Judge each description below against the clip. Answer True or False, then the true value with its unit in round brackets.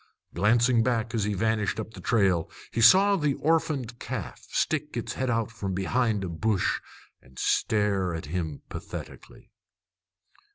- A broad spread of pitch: False (4.3 semitones)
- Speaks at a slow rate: False (150 wpm)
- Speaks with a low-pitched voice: True (110 Hz)